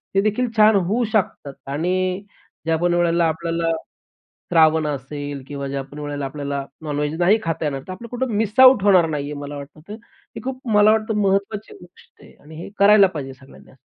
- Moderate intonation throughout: No, wide, 5.9 semitones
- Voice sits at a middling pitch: Yes, medium, 170 Hz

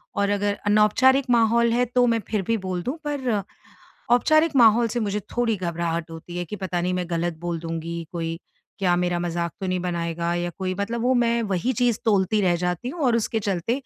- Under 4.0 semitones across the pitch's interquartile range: No, average, 5.2 semitones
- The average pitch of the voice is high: Yes, high, 200 Hz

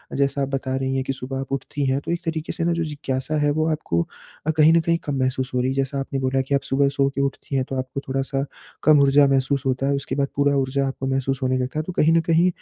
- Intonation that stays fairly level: Yes, narrow, 1.7 semitones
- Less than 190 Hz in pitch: Yes, low, 135 Hz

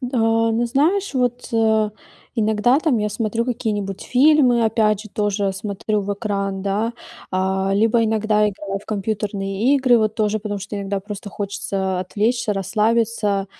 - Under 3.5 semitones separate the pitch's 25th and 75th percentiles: Yes, narrow, 2.6 semitones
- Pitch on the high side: Yes, high, 210 Hz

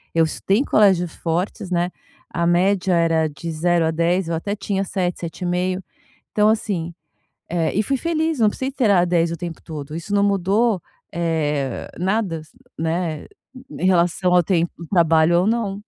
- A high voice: No, medium, 175 Hz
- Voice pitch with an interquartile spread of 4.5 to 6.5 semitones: No, average, 3.2 semitones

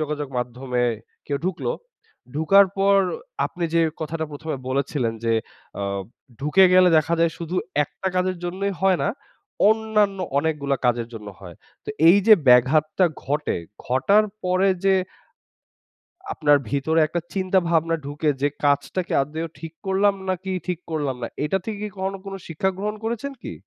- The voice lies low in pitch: No, medium, 165 Hz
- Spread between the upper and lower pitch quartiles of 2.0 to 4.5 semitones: No, average, 4.9 semitones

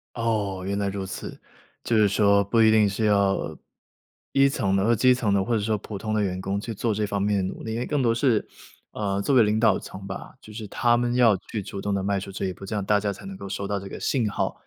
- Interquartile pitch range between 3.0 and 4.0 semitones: No, narrow, 2.5 semitones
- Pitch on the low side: Yes, low, 105 Hz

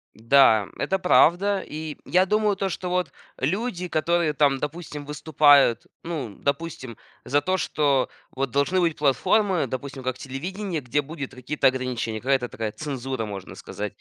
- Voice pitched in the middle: Yes, medium, 145 Hz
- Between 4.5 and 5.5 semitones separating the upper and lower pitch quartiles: Yes, average, 4.9 semitones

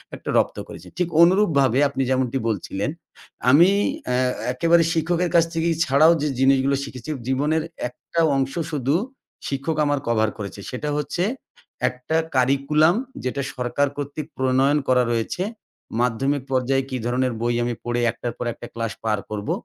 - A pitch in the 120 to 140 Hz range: Yes, low, 135 Hz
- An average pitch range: Yes, average, 3.3 semitones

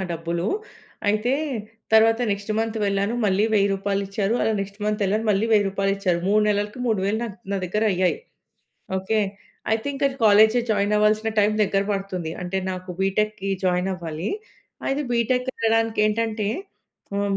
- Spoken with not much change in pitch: Yes, narrow, 2.1 semitones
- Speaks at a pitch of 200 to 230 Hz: Yes, high, 205 Hz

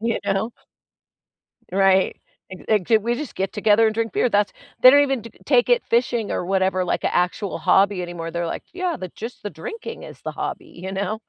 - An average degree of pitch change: Yes, average, 3.9 semitones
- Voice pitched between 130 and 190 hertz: No, high, 205 Hz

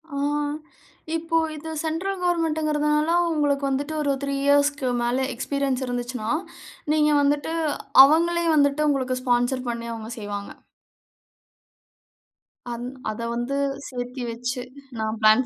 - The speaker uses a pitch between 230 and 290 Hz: Yes, very high, 275 Hz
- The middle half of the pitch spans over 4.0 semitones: No, average, 3.7 semitones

